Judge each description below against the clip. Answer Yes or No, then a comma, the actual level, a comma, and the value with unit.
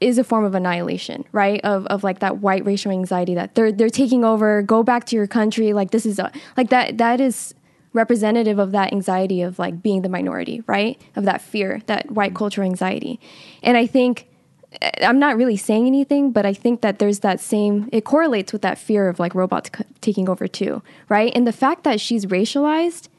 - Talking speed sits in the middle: No, fast, 210 wpm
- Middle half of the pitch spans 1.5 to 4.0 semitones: Yes, average, 3.6 semitones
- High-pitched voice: Yes, high, 215 Hz